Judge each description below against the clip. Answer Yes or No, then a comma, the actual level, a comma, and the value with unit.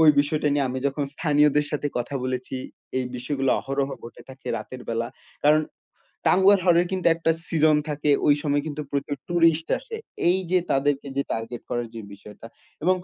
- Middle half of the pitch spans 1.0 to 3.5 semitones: Yes, average, 3.0 semitones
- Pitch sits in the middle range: Yes, medium, 145 Hz